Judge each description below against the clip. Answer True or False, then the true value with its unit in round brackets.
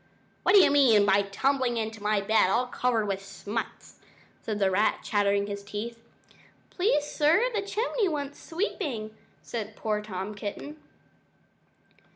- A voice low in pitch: False (220 Hz)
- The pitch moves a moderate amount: False (5.9 semitones)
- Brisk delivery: False (145 wpm)